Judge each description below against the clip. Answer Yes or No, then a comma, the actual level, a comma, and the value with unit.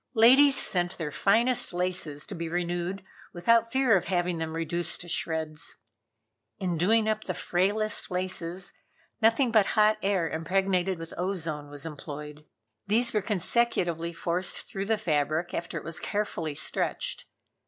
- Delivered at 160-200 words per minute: No, average, 145 wpm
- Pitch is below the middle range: No, medium, 180 Hz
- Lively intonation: No, average, 4.3 semitones